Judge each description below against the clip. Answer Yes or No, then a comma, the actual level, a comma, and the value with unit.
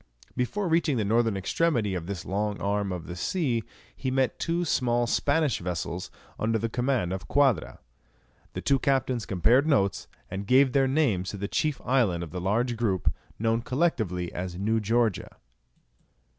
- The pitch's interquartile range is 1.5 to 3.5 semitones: No, wide, 5.6 semitones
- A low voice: Yes, low, 115 Hz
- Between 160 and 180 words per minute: Yes, average, 165 wpm